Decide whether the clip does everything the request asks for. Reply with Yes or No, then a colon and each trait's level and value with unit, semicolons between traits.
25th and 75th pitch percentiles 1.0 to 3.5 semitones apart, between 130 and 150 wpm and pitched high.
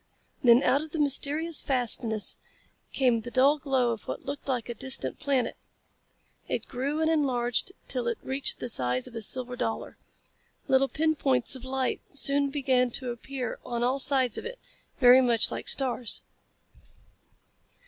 No: narrow, 2.5 semitones; average, 160 wpm; very high, 260 Hz